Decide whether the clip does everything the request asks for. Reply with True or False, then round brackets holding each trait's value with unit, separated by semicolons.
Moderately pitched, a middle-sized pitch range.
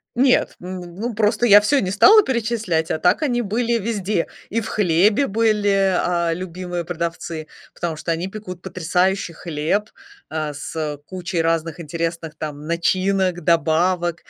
True (180 Hz; 3.9 semitones)